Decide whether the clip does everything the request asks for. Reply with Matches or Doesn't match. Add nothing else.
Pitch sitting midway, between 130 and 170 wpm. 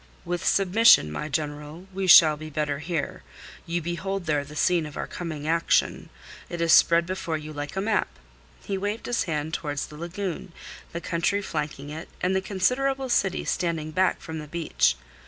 Doesn't match